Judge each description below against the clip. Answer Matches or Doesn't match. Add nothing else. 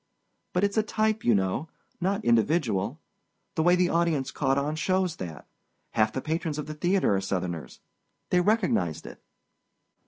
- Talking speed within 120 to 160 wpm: Matches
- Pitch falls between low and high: Matches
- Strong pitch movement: Matches